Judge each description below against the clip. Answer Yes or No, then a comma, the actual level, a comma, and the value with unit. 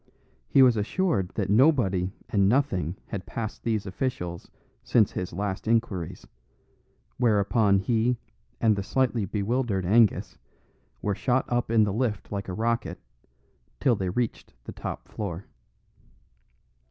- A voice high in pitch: No, low, 105 Hz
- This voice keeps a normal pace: No, slow, 130 wpm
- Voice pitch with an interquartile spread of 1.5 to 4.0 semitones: Yes, average, 3.6 semitones